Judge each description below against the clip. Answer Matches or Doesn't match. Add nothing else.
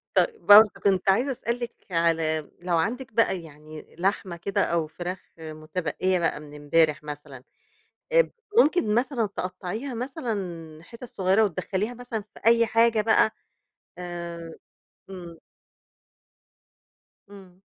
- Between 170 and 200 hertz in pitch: Matches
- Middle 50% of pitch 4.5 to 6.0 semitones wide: Matches